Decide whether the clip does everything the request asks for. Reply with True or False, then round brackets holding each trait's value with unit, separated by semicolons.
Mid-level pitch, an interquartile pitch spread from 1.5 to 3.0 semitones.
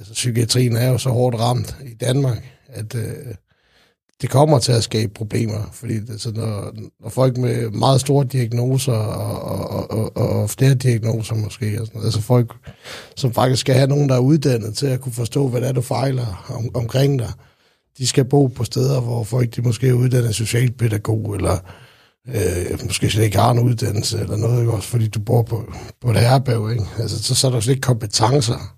False (120 Hz; 2.5 semitones)